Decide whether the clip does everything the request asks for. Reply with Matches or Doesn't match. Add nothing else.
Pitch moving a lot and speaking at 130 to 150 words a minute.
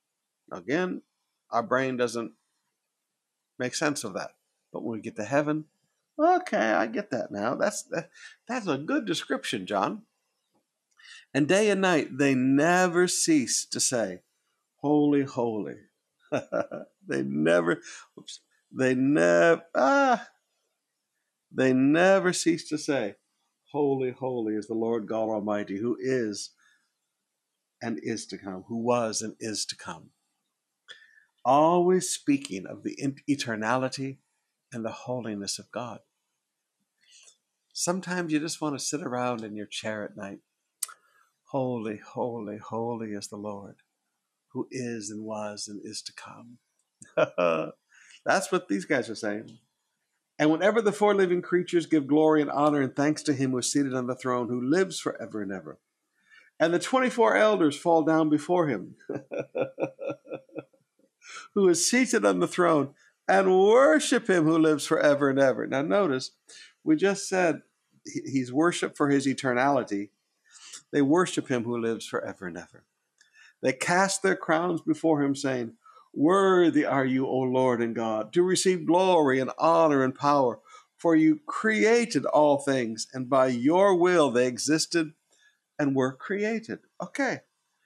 Matches